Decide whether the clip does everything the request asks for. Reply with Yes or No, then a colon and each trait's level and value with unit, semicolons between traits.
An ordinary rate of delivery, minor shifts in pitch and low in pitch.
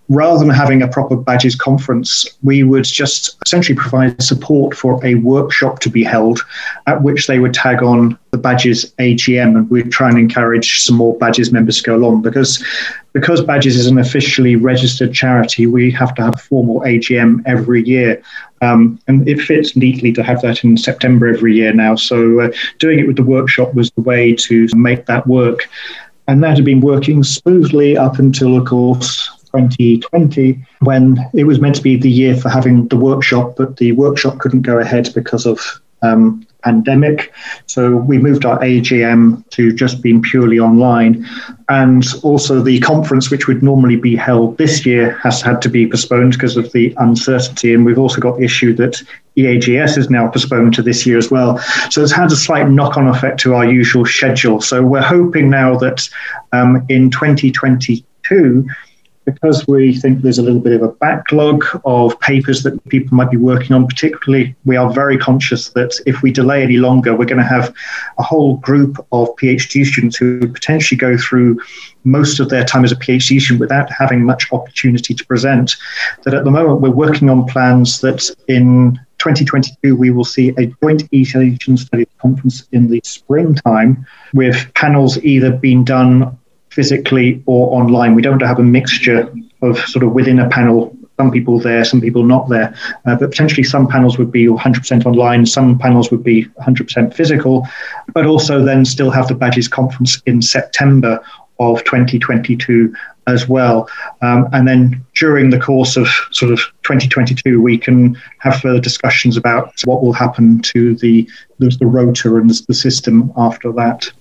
Yes: average, 180 wpm; narrow, 1.9 semitones; low, 125 Hz